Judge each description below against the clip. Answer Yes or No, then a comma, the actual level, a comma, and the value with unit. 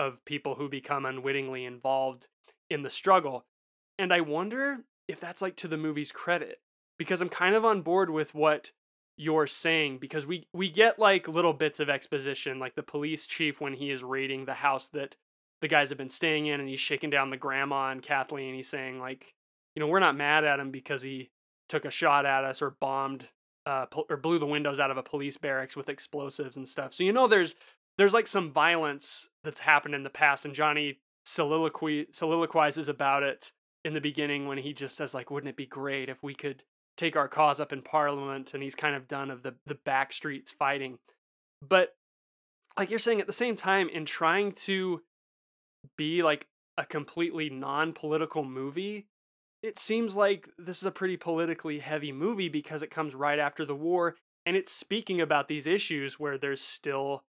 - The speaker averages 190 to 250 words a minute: Yes, average, 200 wpm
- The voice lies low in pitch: No, medium, 150 Hz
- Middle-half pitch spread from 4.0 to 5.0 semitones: No, average, 3.6 semitones